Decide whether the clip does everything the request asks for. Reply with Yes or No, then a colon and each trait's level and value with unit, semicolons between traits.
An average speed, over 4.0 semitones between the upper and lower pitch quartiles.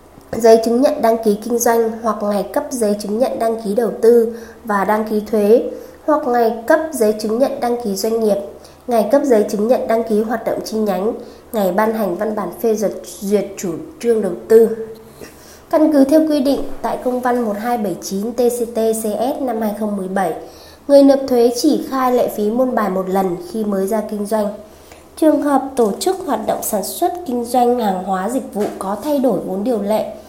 No: average, 200 wpm; average, 3.3 semitones